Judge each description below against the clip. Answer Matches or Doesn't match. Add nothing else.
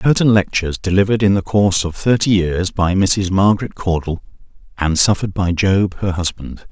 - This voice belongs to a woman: Doesn't match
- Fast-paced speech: Doesn't match